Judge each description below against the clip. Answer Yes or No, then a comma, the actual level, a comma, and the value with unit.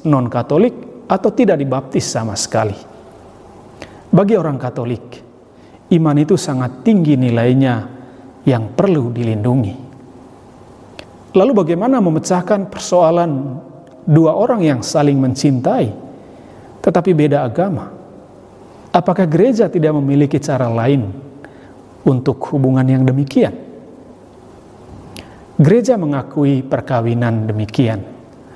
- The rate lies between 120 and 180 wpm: No, average, 90 wpm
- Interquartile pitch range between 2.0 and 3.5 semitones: No, average, 4.8 semitones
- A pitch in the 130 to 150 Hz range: Yes, low, 135 Hz